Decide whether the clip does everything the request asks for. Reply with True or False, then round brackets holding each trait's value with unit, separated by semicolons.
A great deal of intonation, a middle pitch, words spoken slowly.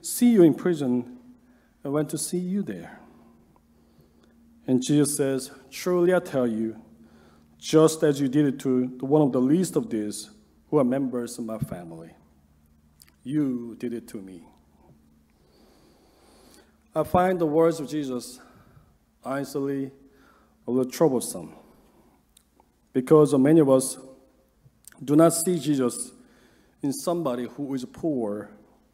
False (5.7 semitones; 130 Hz; 130 wpm)